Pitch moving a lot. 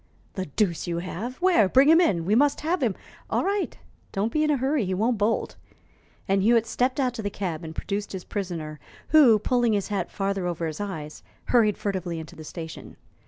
Yes: wide, 5.9 semitones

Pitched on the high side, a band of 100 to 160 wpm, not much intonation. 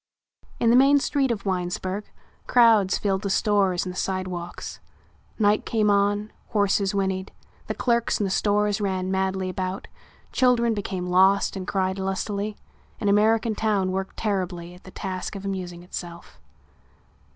Yes: high, 195 Hz; average, 150 wpm; narrow, 2.1 semitones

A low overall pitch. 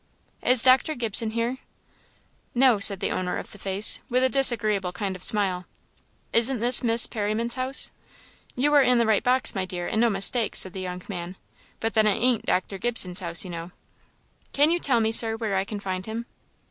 No: high, 220 Hz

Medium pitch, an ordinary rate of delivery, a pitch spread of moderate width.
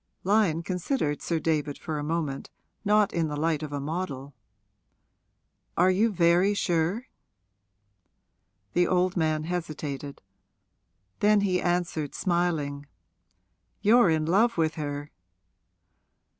No: medium, 165 Hz; slow, 115 wpm; average, 3.5 semitones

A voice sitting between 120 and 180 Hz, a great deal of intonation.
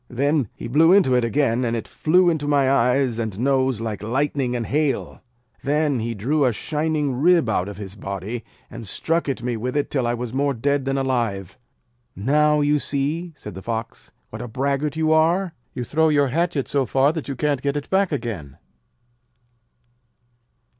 No: low, 135 Hz; average, 4.2 semitones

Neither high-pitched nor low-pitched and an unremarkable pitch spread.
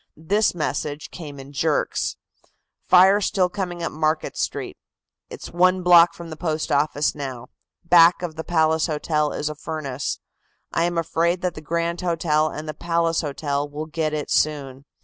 No: medium, 160 Hz; narrow, 2.3 semitones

